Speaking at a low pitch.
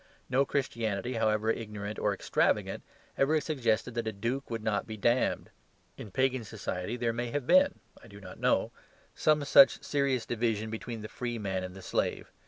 Yes: low, 115 Hz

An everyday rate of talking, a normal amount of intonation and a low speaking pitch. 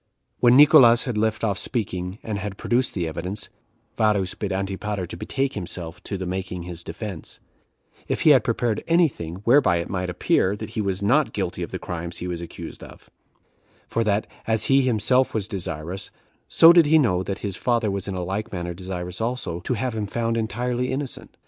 Yes: average, 195 wpm; average, 4.7 semitones; low, 100 Hz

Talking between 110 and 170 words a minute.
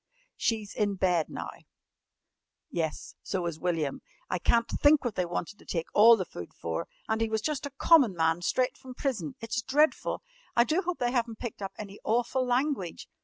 No: average, 195 wpm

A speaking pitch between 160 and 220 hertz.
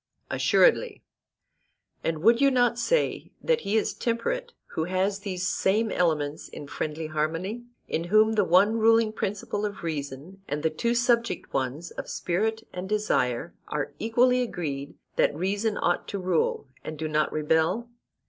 Yes: high, 190 Hz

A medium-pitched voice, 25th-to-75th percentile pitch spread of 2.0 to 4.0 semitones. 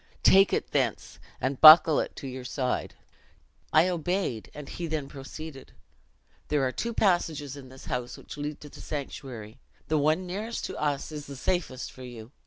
Yes: medium, 145 Hz; average, 3.6 semitones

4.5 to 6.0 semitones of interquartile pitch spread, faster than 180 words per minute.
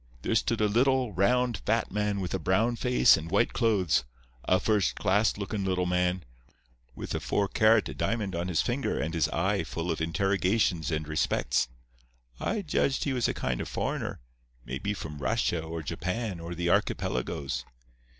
No: average, 5.0 semitones; average, 170 wpm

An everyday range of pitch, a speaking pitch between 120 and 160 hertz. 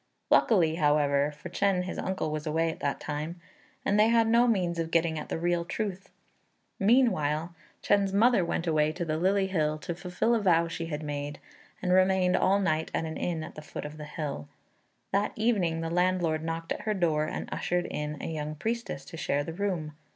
No: average, 3.7 semitones; medium, 170 Hz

